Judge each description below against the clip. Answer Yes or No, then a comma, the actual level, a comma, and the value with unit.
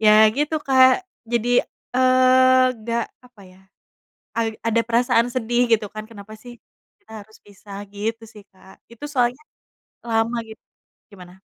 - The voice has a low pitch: No, high, 230 Hz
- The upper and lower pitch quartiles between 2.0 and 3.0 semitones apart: Yes, average, 2.7 semitones